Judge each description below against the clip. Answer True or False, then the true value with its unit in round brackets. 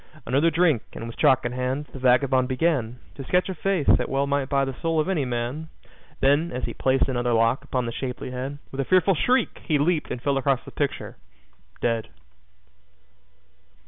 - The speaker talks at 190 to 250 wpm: True (195 wpm)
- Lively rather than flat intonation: False (3.6 semitones)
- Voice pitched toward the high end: False (135 Hz)